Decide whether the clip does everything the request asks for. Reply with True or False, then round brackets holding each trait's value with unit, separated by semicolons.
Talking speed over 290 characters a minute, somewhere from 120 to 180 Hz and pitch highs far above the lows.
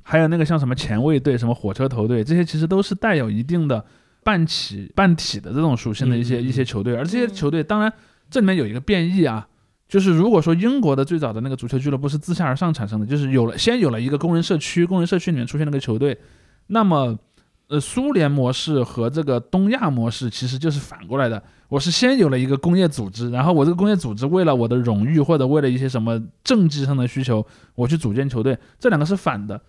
True (370 characters per minute; 140 Hz; 5.8 semitones)